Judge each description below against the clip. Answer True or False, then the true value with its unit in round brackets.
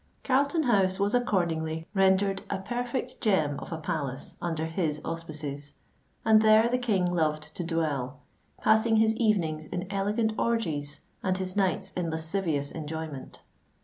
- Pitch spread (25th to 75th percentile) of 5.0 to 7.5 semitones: True (5.4 semitones)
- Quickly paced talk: False (145 wpm)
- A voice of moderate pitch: True (180 Hz)